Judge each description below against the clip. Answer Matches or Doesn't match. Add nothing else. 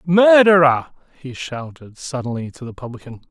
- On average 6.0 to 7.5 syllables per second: Doesn't match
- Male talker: Matches